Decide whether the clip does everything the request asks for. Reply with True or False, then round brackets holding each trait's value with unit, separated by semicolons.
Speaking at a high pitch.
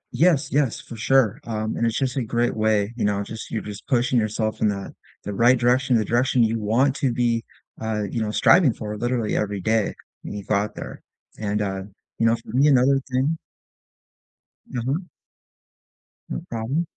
False (115 Hz)